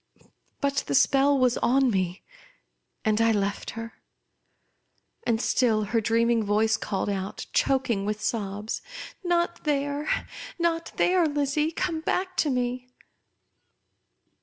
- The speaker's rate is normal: No, slow, 130 wpm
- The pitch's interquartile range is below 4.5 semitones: No, wide, 5.6 semitones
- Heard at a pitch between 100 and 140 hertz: No, high, 245 Hz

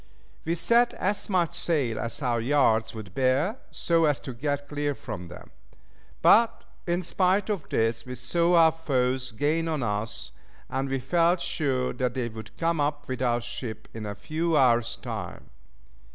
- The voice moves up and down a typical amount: No, wide, 5.9 semitones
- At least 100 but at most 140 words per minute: No, average, 170 wpm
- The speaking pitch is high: No, medium, 140 Hz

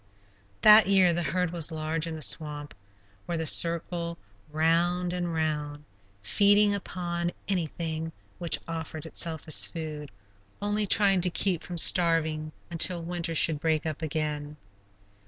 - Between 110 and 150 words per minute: Yes, average, 140 wpm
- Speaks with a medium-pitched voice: Yes, medium, 165 Hz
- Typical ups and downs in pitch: No, narrow, 2.1 semitones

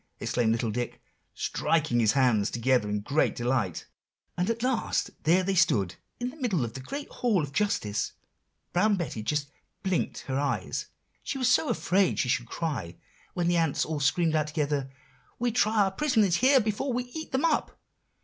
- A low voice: No, medium, 160 Hz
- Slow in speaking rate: No, average, 180 wpm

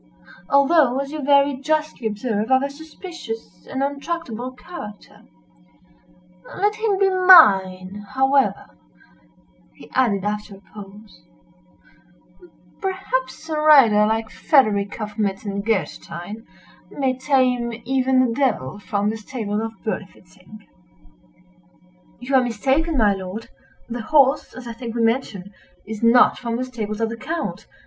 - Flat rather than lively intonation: No, average, 4.9 semitones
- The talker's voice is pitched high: Yes, high, 240 Hz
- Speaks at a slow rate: Yes, slow, 125 wpm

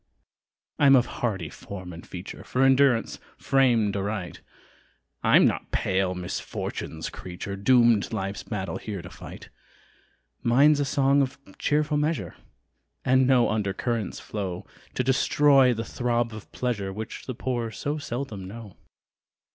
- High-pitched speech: No, low, 115 Hz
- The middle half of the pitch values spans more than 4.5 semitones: Yes, average, 5.1 semitones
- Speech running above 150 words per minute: No, slow, 135 wpm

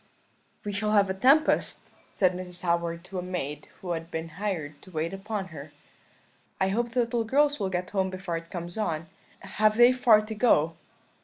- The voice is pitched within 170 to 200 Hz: Yes, high, 190 Hz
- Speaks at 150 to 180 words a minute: No, average, 190 wpm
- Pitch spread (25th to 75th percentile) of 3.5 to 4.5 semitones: Yes, average, 4.1 semitones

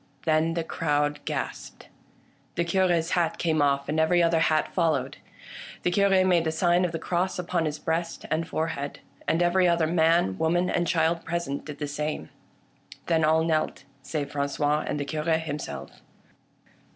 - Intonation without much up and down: Yes, narrow, 2.3 semitones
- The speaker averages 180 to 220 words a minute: No, average, 170 wpm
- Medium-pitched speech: Yes, medium, 160 Hz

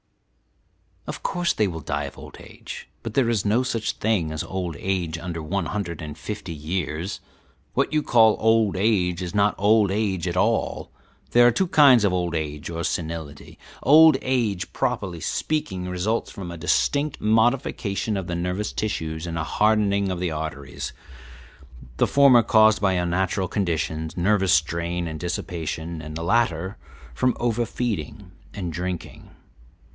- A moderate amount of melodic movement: Yes, average, 4.6 semitones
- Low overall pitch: Yes, very low, 95 Hz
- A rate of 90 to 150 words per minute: No, average, 160 wpm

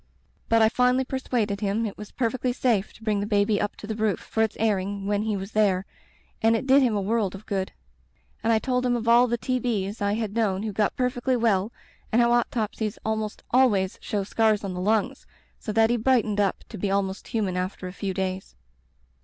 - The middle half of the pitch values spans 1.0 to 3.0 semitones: Yes, average, 2.7 semitones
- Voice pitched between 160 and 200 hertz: No, high, 215 Hz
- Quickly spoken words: Yes, fast, 220 wpm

